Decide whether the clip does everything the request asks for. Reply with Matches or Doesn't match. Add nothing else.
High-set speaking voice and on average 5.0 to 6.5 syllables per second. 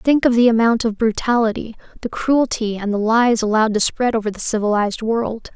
Matches